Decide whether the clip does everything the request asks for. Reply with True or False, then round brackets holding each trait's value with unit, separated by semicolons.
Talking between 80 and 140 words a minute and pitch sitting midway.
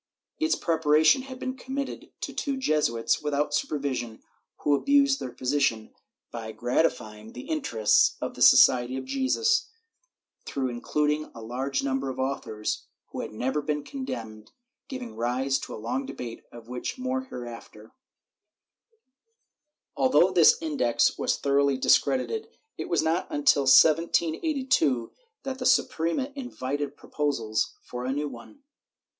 True (135 wpm; 145 Hz)